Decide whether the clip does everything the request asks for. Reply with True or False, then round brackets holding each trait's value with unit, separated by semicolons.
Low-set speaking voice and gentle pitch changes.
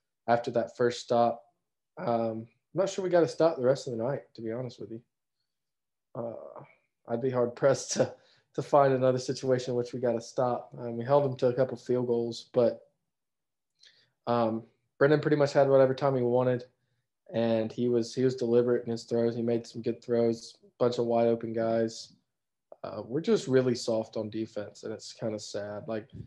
True (120 Hz; 2.2 semitones)